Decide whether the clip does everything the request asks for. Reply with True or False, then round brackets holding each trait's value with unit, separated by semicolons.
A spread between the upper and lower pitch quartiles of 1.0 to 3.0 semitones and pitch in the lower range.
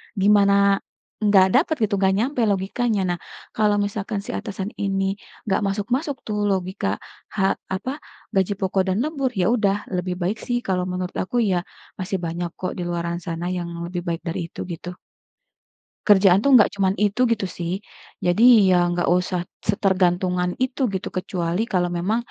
False (2.4 semitones; 195 Hz)